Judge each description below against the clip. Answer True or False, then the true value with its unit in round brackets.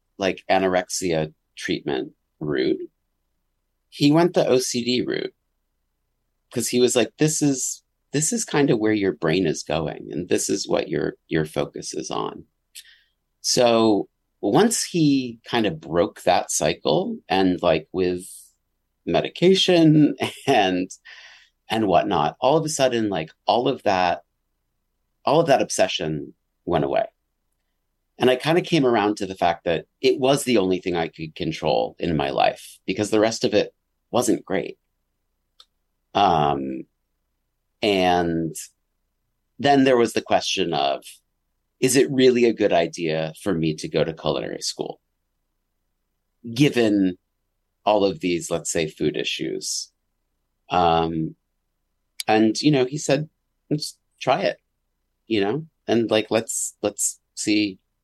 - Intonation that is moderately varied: False (7.3 semitones)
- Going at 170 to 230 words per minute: False (140 wpm)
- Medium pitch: False (110 Hz)